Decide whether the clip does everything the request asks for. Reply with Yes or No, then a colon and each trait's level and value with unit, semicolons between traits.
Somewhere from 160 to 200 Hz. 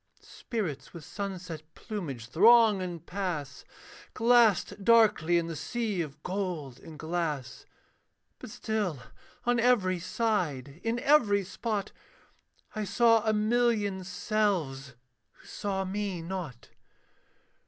Yes: high, 190 Hz